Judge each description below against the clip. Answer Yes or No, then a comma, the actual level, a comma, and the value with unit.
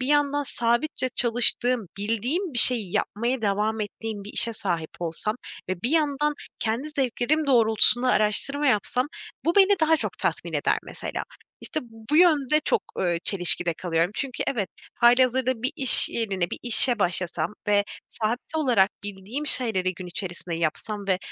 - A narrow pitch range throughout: No, average, 5.2 semitones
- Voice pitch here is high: Yes, high, 230 Hz